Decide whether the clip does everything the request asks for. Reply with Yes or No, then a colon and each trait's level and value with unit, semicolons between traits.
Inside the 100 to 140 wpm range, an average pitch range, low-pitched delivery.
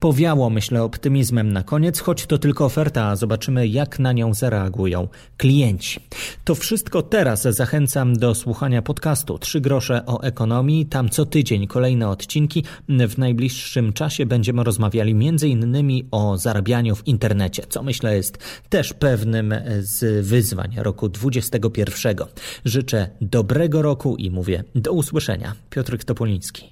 Yes: average, 135 wpm; average, 4.2 semitones; low, 120 Hz